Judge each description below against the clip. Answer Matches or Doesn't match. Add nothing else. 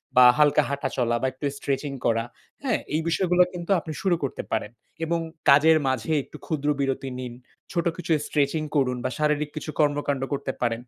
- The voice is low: Doesn't match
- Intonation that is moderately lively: Matches